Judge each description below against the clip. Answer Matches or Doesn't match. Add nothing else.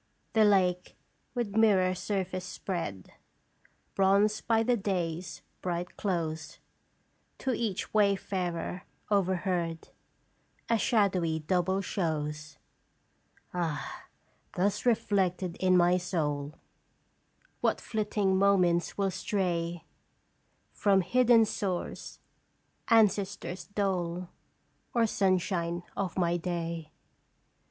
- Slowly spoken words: Matches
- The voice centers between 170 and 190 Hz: Matches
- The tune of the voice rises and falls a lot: Doesn't match